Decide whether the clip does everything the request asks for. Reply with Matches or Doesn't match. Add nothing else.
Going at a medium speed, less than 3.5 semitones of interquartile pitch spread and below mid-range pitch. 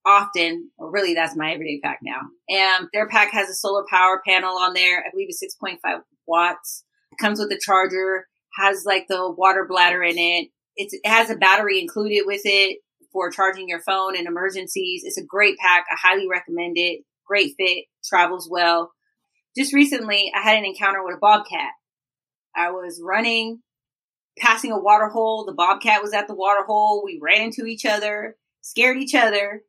Doesn't match